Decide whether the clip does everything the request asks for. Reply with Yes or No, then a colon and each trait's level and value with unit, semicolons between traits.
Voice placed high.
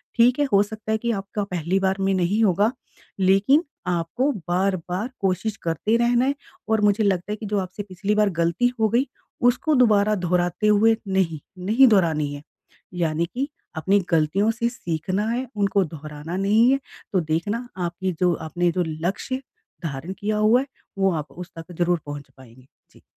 Yes: high, 195 Hz